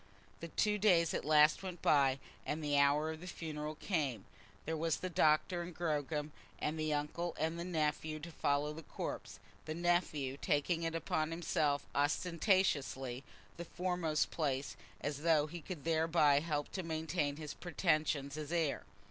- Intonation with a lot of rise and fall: No, narrow, 2.4 semitones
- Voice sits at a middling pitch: Yes, medium, 155 Hz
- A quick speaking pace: No, average, 160 wpm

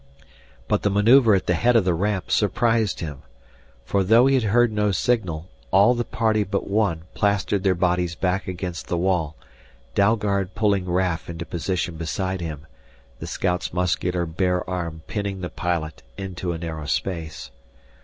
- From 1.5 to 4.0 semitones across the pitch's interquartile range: Yes, average, 3.2 semitones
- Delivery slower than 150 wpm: No, average, 165 wpm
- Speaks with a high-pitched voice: No, very low, 95 Hz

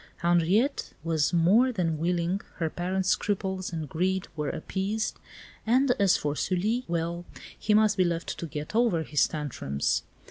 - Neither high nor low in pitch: Yes, medium, 180 Hz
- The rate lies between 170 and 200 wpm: No, average, 150 wpm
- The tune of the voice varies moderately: Yes, average, 3.8 semitones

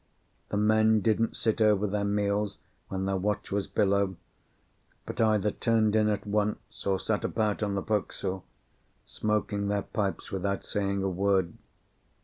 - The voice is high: No, low, 105 Hz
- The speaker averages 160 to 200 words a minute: No, average, 150 wpm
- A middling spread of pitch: No, narrow, 1.5 semitones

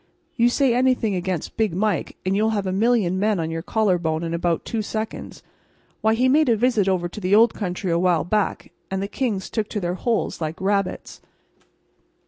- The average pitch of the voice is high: Yes, high, 200 Hz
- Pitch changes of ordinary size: Yes, average, 3.8 semitones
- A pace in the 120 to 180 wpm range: No, average, 195 wpm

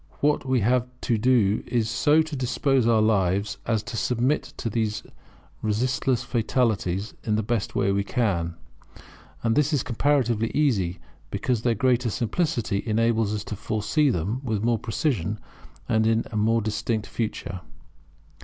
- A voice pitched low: Yes, low, 115 Hz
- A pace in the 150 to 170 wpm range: Yes, average, 155 wpm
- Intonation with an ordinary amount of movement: Yes, average, 3.1 semitones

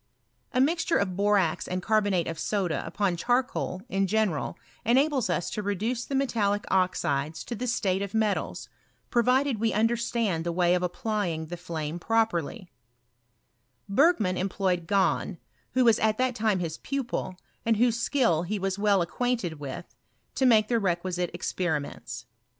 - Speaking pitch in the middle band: No, high, 200 Hz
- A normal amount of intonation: Yes, average, 4.7 semitones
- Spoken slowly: No, average, 155 wpm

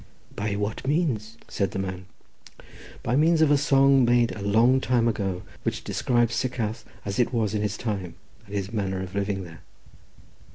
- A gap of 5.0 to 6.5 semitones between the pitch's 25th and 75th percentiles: No, average, 3.9 semitones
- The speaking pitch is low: Yes, low, 110 Hz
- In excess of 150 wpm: Yes, average, 175 wpm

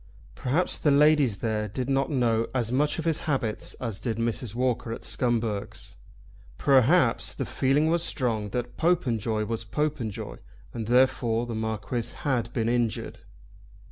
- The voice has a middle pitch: No, low, 120 Hz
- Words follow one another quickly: No, average, 150 wpm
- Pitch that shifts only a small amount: No, average, 3.4 semitones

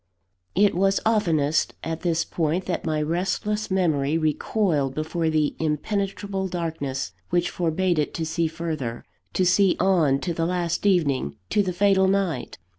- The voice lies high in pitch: No, medium, 170 Hz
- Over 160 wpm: No, average, 150 wpm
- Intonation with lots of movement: No, average, 3.6 semitones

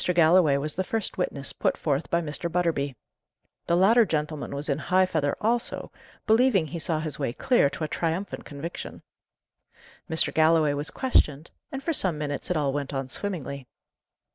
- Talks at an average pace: Yes, average, 170 wpm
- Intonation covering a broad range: No, average, 4.3 semitones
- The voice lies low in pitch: No, medium, 160 Hz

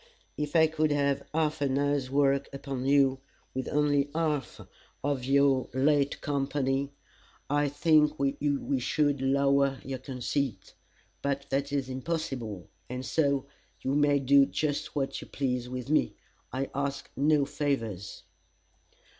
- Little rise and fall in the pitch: Yes, narrow, 1.5 semitones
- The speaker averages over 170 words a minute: No, slow, 135 wpm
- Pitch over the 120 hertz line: Yes, medium, 140 Hz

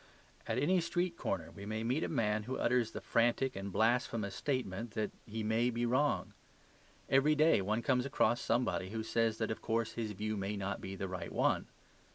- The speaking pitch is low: Yes, low, 115 Hz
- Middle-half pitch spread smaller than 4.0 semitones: Yes, average, 3.1 semitones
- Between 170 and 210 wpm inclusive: Yes, average, 200 wpm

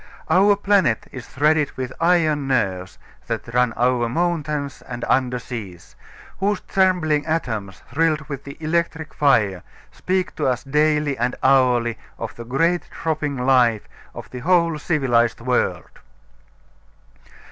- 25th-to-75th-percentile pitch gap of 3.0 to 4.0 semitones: No, average, 4.9 semitones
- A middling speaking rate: No, slow, 130 wpm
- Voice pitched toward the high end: No, medium, 140 Hz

